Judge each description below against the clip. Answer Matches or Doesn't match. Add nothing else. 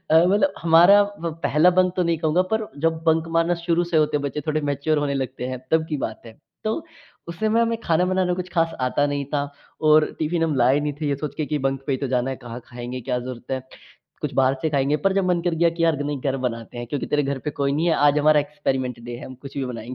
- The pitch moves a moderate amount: Matches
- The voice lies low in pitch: Doesn't match